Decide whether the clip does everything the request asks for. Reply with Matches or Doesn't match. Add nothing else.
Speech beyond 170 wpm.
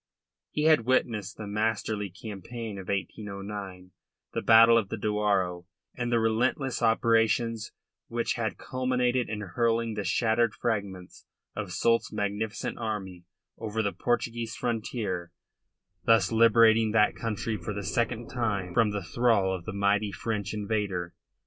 Doesn't match